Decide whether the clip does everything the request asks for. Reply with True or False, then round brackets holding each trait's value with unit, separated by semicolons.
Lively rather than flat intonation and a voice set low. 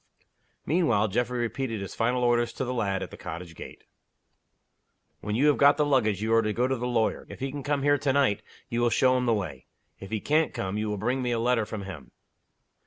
False (3.8 semitones; 120 Hz)